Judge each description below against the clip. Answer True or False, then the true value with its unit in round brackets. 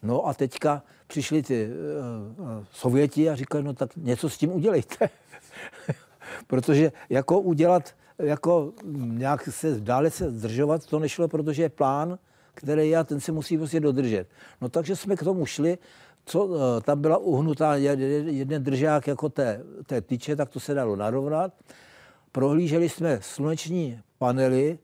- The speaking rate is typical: True (150 wpm)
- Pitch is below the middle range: False (150 Hz)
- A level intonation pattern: False (3.2 semitones)